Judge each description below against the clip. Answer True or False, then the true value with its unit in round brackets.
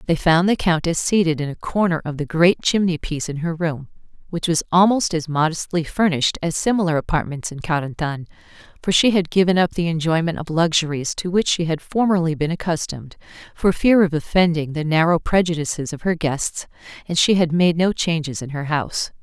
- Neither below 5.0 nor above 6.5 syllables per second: True (5.6 syllables/s)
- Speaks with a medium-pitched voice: True (165 Hz)